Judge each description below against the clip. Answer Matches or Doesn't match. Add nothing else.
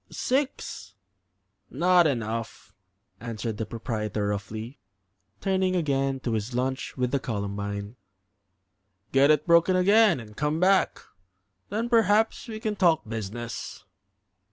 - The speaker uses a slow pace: Matches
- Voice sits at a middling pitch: Doesn't match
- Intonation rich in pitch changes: Matches